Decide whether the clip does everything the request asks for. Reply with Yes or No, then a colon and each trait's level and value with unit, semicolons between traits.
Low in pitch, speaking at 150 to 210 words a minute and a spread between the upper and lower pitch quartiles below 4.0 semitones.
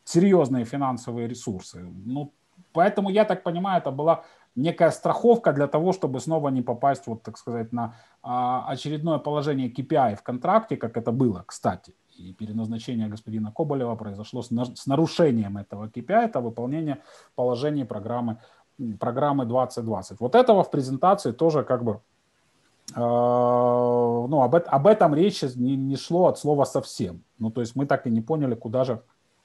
No: low, 130 Hz; fast, 155 wpm; average, 4.3 semitones